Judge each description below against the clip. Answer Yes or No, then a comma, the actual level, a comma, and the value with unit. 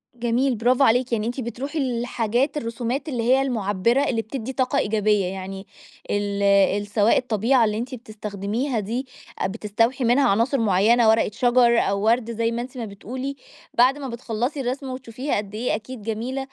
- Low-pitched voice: No, high, 235 Hz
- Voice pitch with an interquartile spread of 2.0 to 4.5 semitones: Yes, average, 3.1 semitones